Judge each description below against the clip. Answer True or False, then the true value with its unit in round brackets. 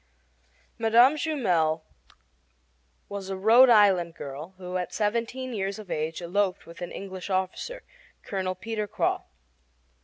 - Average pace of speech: False (125 wpm)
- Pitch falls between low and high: False (195 Hz)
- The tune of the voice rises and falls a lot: False (3.9 semitones)